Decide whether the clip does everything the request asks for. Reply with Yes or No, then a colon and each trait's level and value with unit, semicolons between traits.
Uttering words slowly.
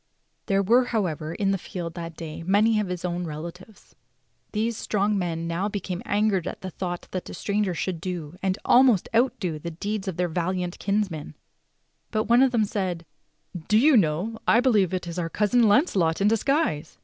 No: average, 190 wpm